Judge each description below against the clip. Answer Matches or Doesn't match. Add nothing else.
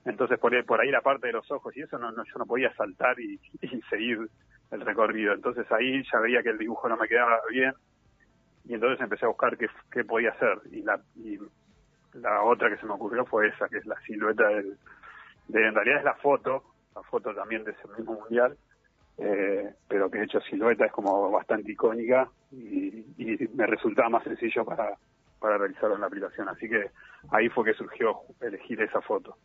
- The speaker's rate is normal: Doesn't match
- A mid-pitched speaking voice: Doesn't match